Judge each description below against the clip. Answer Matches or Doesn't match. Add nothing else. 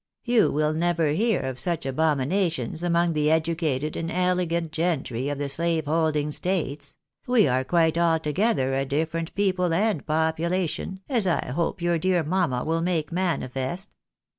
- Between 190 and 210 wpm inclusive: Doesn't match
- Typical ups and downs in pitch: Matches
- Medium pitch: Matches